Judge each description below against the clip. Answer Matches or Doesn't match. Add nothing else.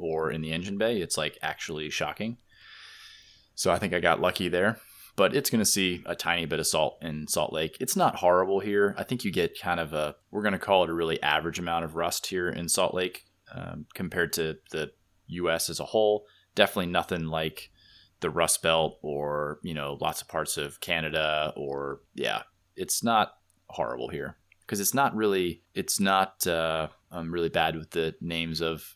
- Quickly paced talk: Doesn't match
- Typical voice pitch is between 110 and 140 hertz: Doesn't match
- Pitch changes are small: Doesn't match